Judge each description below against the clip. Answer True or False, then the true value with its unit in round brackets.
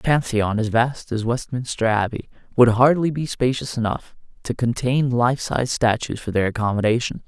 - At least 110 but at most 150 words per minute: False (165 wpm)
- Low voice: True (120 Hz)